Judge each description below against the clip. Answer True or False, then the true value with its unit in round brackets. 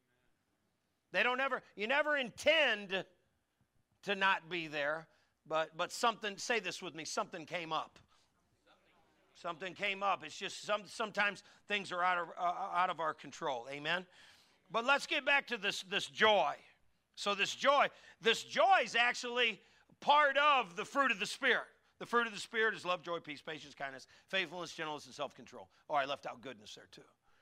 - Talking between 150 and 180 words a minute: True (175 wpm)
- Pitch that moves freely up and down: True (6.3 semitones)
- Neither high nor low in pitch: False (195 Hz)